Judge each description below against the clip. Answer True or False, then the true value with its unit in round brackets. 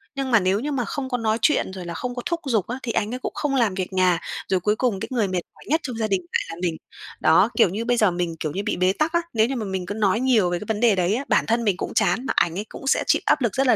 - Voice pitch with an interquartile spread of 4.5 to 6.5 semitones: True (5.1 semitones)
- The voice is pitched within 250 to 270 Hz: False (220 Hz)